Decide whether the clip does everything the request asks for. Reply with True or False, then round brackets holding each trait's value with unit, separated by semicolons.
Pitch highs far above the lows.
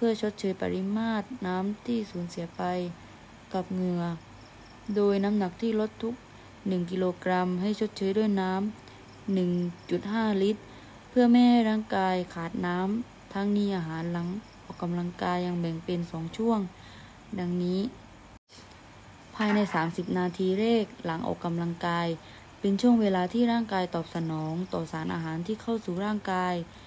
False (3.5 semitones)